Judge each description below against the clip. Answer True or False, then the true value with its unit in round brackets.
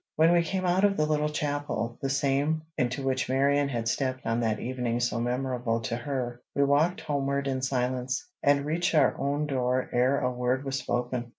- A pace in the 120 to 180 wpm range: False (195 wpm)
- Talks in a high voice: False (135 Hz)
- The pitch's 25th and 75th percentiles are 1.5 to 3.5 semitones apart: True (2.7 semitones)